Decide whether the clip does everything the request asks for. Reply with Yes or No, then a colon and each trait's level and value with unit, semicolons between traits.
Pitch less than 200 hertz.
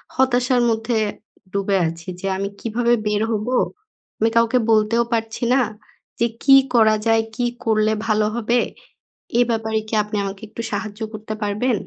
No: high, 220 Hz